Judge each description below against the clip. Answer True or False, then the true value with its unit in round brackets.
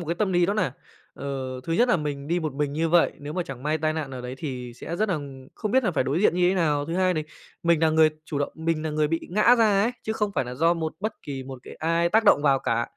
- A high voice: False (160 Hz)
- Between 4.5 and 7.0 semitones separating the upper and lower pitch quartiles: False (4.0 semitones)